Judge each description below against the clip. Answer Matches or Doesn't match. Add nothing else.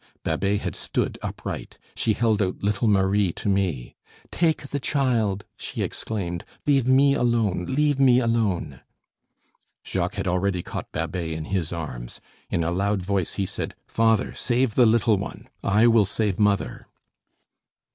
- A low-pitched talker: Matches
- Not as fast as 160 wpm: Matches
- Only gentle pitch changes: Doesn't match